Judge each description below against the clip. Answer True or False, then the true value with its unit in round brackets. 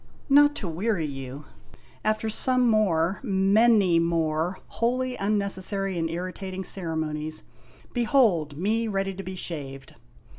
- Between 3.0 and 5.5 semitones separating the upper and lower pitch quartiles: True (4.9 semitones)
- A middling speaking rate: False (120 wpm)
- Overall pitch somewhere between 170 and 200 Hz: True (190 Hz)